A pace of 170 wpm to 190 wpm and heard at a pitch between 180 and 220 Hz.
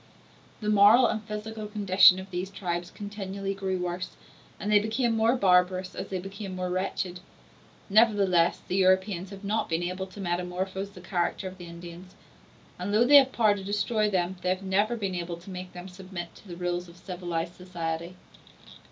Yes: average, 185 wpm; high, 190 Hz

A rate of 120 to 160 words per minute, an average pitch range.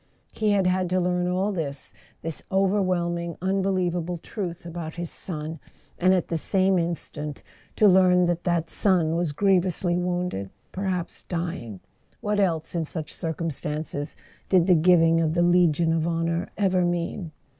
No: average, 155 wpm; narrow, 2.0 semitones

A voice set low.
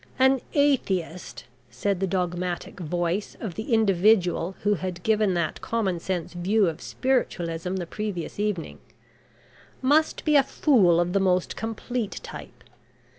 No: high, 190 Hz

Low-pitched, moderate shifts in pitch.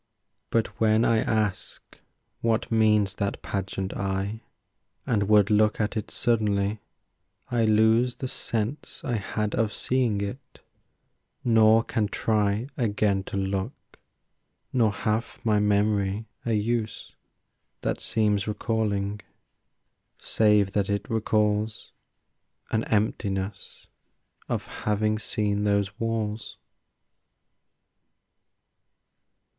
No: low, 105 Hz; narrow, 1.7 semitones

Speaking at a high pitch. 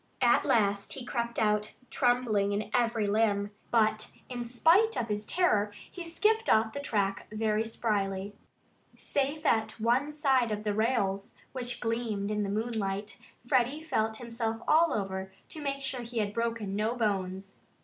Yes: high, 225 Hz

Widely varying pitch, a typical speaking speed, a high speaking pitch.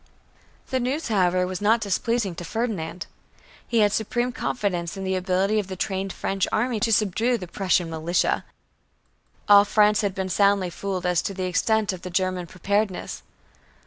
No: average, 2.8 semitones; average, 170 wpm; high, 195 Hz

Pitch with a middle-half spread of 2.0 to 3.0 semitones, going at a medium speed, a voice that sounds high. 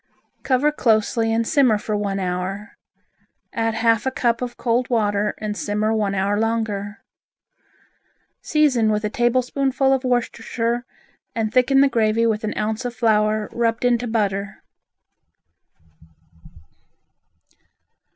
No: narrow, 2.5 semitones; slow, 120 wpm; high, 225 Hz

